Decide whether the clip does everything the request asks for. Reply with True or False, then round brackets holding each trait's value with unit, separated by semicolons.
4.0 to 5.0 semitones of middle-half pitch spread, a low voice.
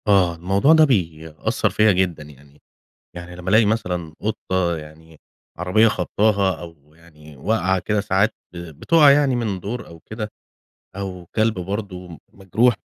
True (4.4 semitones; 95 Hz)